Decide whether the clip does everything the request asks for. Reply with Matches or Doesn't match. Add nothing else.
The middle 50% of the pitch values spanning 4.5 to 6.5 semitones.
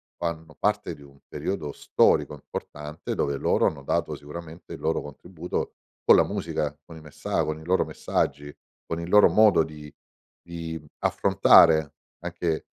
Doesn't match